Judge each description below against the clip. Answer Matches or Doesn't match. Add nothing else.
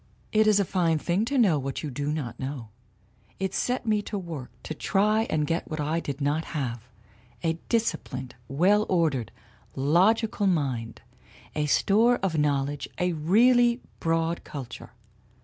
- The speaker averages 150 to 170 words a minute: Matches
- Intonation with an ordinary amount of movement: Doesn't match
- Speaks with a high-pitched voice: Doesn't match